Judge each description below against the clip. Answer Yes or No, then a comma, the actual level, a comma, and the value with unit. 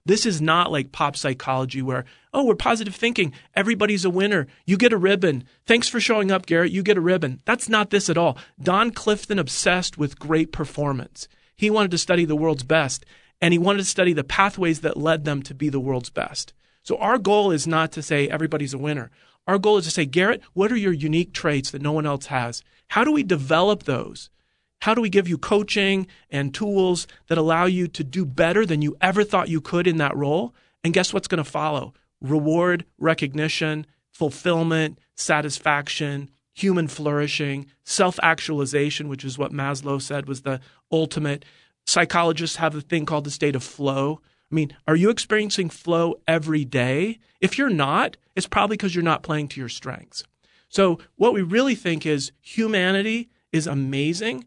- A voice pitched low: No, medium, 160 Hz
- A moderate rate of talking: Yes, average, 190 wpm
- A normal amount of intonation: Yes, average, 4.9 semitones